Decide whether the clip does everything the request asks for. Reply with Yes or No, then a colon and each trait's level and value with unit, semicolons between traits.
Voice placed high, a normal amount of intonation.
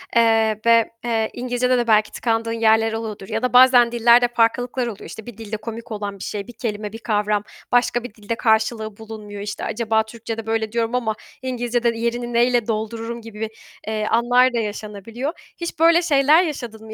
No: high, 230 Hz; narrow, 1.8 semitones